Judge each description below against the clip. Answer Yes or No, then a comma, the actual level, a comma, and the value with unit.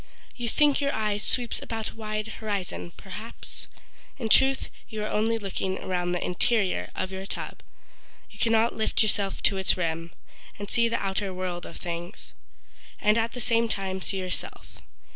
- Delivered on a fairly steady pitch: No, average, 3.3 semitones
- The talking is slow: No, average, 170 wpm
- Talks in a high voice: Yes, high, 210 Hz